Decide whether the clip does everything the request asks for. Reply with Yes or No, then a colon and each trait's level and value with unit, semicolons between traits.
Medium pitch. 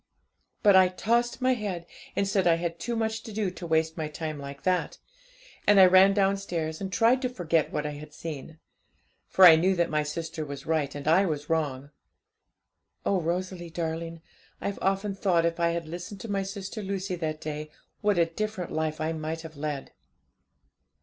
Yes: medium, 170 Hz